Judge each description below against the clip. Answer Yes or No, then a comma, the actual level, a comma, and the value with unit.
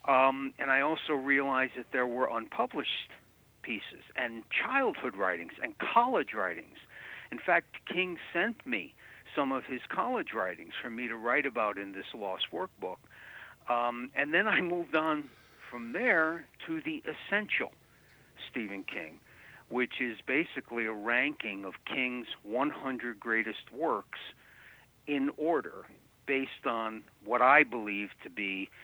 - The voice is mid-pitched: No, low, 130 Hz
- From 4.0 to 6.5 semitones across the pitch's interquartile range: Yes, average, 4.5 semitones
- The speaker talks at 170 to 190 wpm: No, average, 140 wpm